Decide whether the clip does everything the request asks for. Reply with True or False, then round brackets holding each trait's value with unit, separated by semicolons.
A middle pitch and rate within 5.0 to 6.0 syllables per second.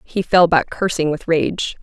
False (170 Hz; 4.2 syllables/s)